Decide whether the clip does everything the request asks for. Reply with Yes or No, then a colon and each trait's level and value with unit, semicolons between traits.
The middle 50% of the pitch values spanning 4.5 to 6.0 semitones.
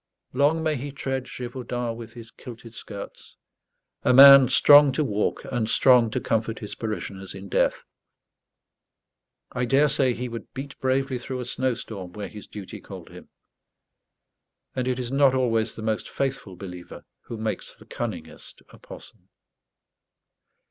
No: average, 3.3 semitones